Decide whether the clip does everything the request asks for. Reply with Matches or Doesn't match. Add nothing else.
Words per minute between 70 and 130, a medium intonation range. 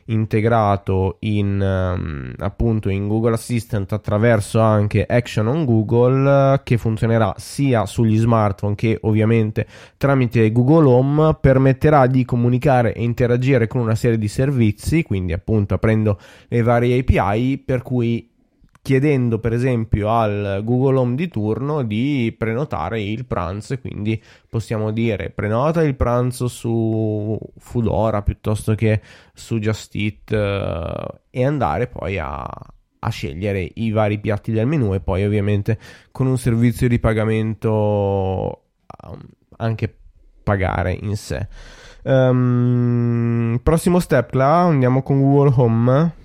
Matches